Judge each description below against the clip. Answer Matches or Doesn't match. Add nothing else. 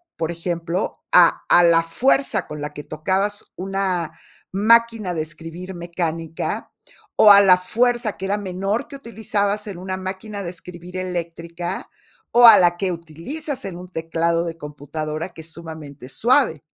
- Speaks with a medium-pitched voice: Matches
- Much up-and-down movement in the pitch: Doesn't match